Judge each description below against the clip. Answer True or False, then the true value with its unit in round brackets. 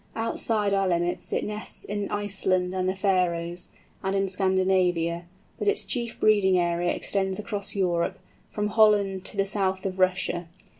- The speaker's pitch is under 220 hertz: True (190 Hz)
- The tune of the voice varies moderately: False (2.1 semitones)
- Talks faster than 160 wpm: False (155 wpm)